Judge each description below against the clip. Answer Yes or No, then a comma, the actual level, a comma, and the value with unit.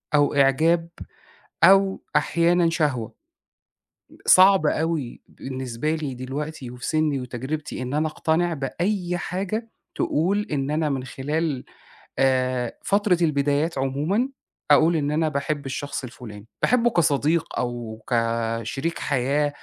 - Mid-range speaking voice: Yes, medium, 150 Hz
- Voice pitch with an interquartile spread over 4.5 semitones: No, average, 4.2 semitones